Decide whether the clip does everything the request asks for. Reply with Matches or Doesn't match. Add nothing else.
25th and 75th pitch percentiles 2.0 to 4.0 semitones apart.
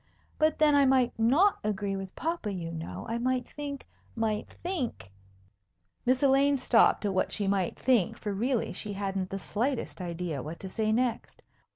Doesn't match